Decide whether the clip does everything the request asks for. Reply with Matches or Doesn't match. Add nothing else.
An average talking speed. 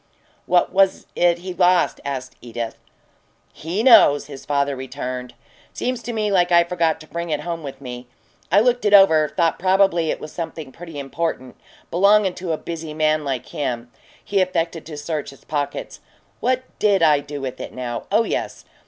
Matches